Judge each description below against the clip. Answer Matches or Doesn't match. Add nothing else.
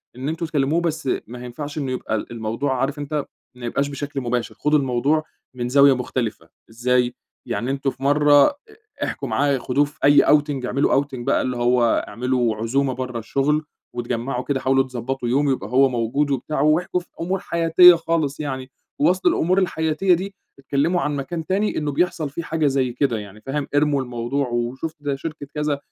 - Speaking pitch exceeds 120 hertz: Matches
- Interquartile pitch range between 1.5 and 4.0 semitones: Matches